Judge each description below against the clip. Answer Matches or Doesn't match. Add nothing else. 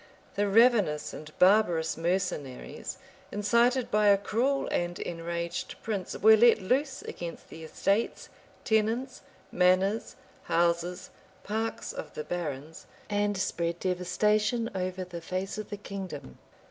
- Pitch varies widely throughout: Doesn't match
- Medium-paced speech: Doesn't match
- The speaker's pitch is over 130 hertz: Matches